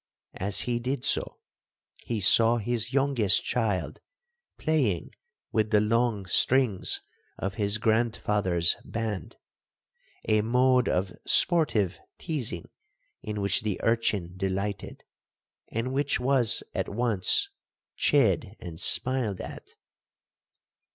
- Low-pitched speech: Yes, low, 110 Hz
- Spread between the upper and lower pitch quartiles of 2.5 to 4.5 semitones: Yes, average, 3.7 semitones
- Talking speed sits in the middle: No, slow, 105 wpm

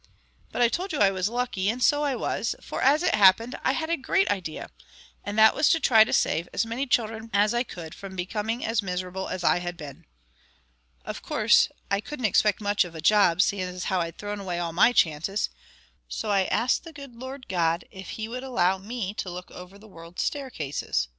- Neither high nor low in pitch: No, high, 205 Hz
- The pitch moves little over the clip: No, average, 5.1 semitones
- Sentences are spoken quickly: Yes, fast, 215 wpm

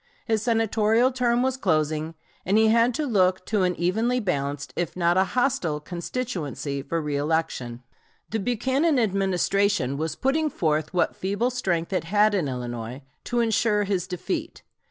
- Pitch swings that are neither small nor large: No, wide, 6.5 semitones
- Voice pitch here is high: Yes, high, 195 Hz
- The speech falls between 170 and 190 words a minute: No, average, 155 wpm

